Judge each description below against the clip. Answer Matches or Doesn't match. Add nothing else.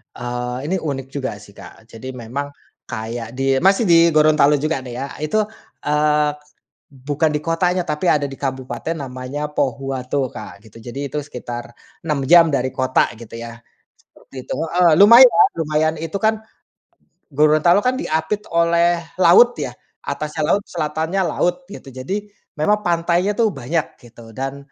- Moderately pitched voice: Matches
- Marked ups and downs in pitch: Doesn't match